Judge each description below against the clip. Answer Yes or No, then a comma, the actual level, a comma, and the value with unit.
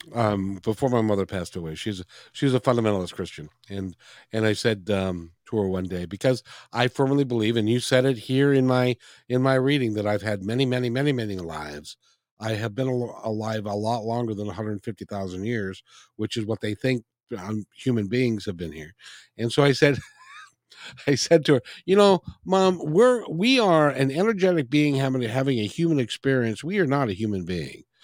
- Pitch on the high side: No, low, 115 Hz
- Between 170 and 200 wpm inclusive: Yes, average, 195 wpm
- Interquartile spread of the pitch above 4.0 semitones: Yes, average, 4.7 semitones